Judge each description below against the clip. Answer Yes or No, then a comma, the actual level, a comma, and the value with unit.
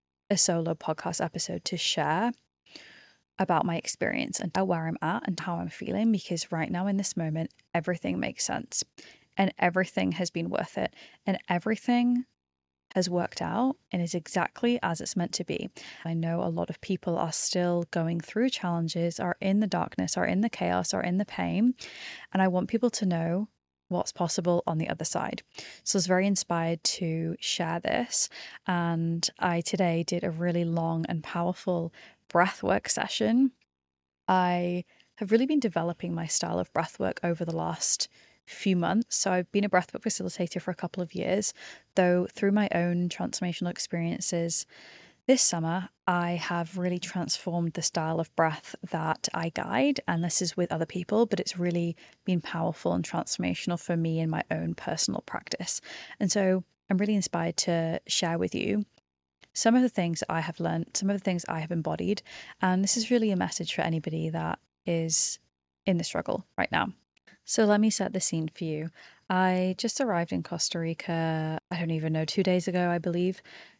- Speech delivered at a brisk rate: No, average, 180 wpm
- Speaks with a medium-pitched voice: Yes, medium, 175 Hz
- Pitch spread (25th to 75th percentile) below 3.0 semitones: Yes, narrow, 2.4 semitones